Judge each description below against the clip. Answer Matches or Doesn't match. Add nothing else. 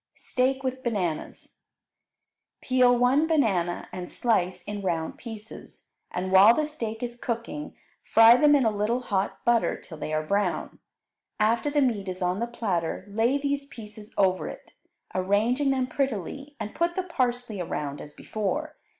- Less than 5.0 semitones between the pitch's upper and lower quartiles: Doesn't match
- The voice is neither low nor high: Doesn't match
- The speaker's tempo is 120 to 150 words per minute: Doesn't match